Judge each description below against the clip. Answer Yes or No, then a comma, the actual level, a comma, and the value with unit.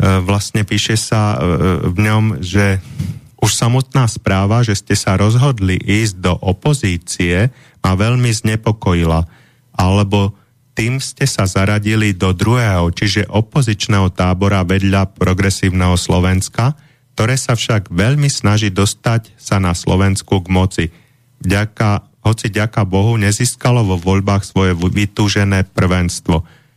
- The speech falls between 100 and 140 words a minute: Yes, average, 120 wpm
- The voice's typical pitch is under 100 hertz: No, low, 105 Hz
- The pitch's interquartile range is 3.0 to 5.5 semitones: Yes, average, 3.4 semitones